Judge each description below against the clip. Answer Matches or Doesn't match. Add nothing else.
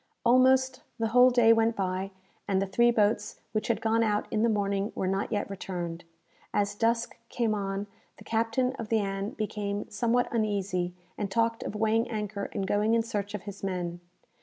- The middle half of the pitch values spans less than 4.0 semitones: Matches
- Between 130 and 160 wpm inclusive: Doesn't match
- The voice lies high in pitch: Matches